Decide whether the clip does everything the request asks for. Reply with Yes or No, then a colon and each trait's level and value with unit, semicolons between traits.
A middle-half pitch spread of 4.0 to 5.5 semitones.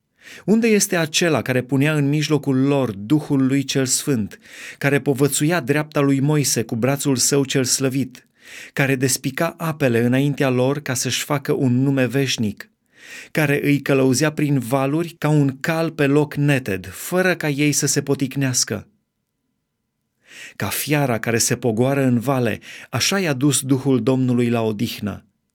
No: narrow, 2.4 semitones